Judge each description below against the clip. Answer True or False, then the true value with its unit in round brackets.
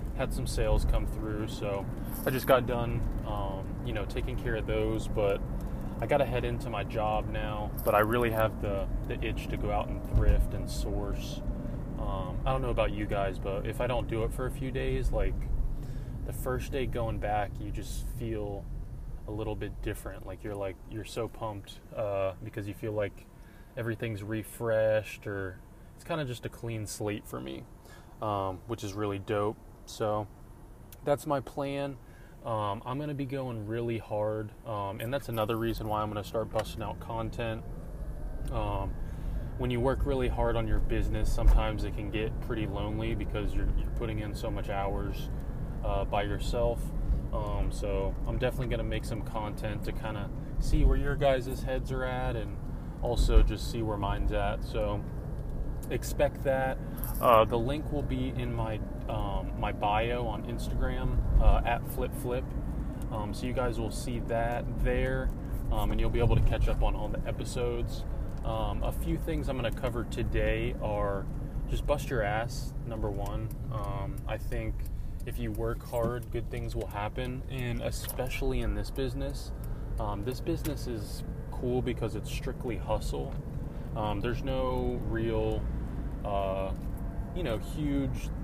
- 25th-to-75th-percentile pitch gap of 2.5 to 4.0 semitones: True (3.2 semitones)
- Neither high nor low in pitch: False (115 Hz)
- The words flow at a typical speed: True (180 wpm)